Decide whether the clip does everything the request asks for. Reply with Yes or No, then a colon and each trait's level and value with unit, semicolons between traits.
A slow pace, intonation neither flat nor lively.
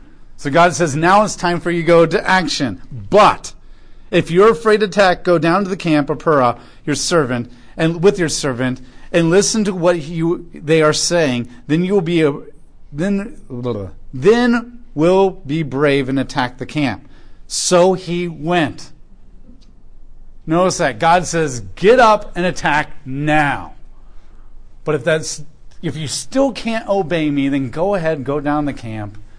No: average, 165 wpm; average, 4.5 semitones